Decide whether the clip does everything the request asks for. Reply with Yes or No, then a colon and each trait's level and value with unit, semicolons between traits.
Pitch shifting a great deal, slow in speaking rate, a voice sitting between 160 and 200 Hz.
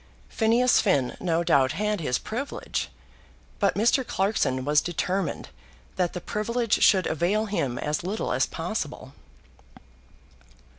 Yes: wide, 6.2 semitones; slow, 120 wpm; medium, 185 Hz